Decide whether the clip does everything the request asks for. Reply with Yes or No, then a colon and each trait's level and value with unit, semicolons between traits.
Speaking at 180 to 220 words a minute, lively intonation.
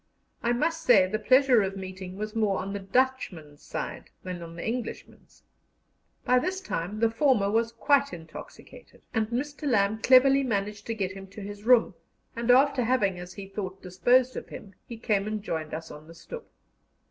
No: average, 185 wpm; average, 4.7 semitones